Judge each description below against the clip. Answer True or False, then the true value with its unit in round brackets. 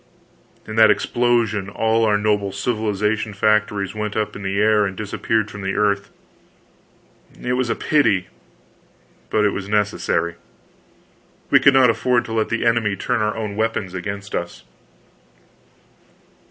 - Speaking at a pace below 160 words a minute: True (145 wpm)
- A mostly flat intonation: True (1.8 semitones)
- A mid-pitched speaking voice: False (105 Hz)